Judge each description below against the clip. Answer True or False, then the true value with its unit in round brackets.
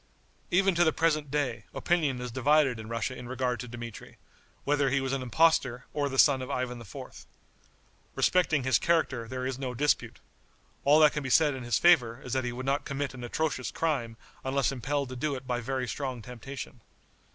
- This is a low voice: True (130 Hz)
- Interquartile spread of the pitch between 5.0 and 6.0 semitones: False (2.9 semitones)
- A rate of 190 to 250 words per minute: True (195 wpm)